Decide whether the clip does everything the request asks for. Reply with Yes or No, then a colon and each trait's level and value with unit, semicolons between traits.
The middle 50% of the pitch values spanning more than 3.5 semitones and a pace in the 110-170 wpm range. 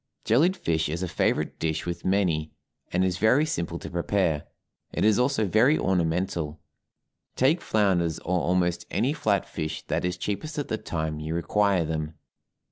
Yes: average, 4.4 semitones; average, 165 wpm